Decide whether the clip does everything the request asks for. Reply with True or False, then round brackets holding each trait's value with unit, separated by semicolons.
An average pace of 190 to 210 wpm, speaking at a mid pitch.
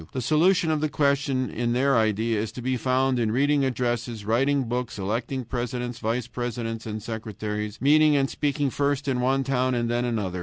False (200 wpm; 125 Hz)